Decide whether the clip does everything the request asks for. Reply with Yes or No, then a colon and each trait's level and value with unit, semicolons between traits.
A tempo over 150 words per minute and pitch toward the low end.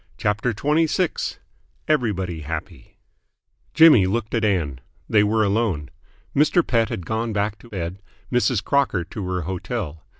No: slow, 135 wpm; low, 105 Hz